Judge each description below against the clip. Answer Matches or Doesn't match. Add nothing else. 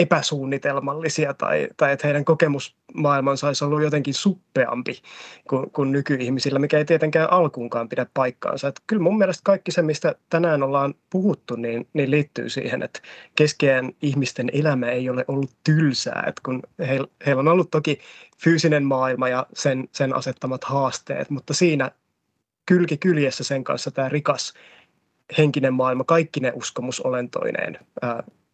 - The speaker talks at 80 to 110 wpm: Doesn't match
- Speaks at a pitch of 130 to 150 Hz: Matches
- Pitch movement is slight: Doesn't match